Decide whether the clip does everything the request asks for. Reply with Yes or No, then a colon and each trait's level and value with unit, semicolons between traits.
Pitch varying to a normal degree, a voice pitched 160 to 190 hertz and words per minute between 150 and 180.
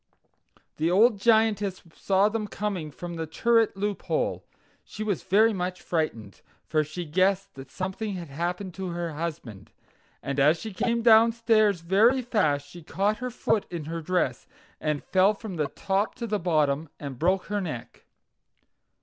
Yes: average, 4.8 semitones; medium, 185 Hz; average, 160 wpm